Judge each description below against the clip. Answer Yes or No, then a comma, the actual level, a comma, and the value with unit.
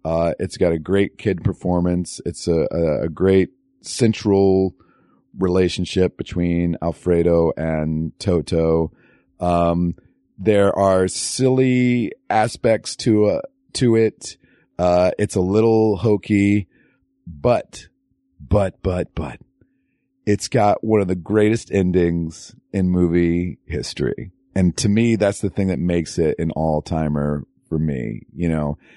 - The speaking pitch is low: Yes, very low, 90 Hz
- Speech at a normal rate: No, slow, 125 wpm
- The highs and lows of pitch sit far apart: No, average, 3.6 semitones